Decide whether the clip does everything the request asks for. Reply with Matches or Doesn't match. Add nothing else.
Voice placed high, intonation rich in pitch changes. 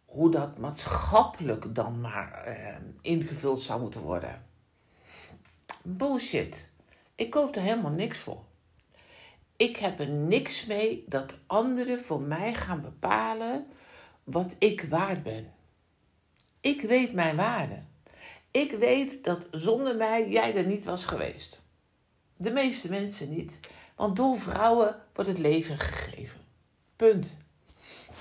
Matches